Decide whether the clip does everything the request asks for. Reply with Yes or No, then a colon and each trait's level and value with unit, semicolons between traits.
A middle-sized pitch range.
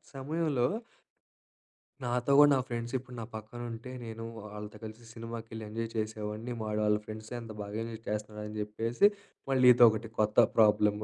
No: narrow, 2.0 semitones